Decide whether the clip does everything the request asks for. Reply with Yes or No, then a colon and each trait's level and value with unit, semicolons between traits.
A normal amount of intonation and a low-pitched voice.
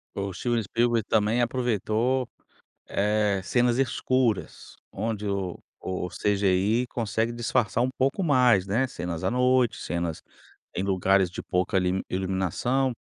Yes: average, 4.3 semitones; low, 110 Hz